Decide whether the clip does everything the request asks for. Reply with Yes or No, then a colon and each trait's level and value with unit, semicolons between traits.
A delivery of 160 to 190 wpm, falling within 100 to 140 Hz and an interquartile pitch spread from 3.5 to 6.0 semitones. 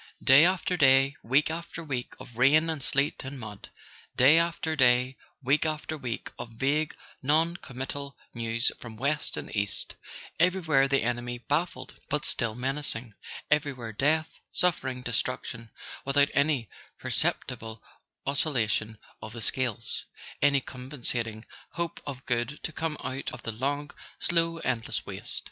No: average, 140 wpm; low, 135 Hz; average, 3.9 semitones